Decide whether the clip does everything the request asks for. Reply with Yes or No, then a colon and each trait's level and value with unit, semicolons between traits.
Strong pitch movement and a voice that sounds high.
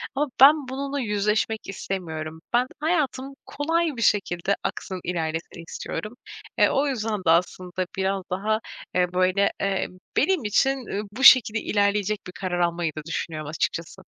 Yes: wide, 6.3 semitones; high, 200 Hz